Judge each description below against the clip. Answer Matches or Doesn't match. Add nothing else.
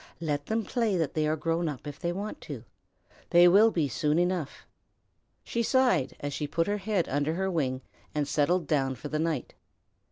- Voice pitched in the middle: Matches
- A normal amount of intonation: Matches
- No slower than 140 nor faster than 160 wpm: Doesn't match